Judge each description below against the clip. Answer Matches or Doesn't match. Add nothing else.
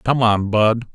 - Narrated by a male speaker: Matches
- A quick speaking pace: Doesn't match